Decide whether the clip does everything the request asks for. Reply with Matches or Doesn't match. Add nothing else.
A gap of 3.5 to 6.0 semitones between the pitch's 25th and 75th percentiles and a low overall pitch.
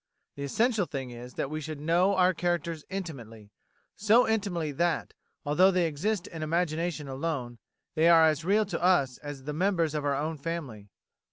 Doesn't match